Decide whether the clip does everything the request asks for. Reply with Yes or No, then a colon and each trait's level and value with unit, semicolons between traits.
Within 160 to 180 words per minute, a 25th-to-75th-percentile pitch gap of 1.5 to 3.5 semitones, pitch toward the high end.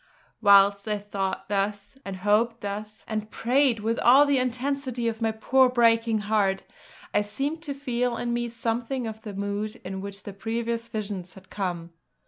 Yes: average, 170 wpm; average, 2.9 semitones; high, 220 Hz